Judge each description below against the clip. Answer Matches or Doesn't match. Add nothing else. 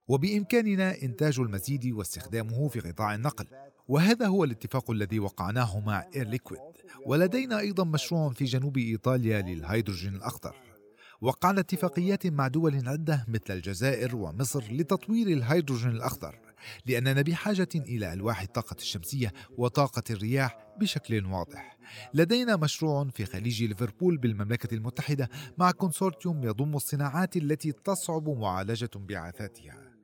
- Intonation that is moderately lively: Doesn't match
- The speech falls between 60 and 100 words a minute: Doesn't match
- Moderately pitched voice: Doesn't match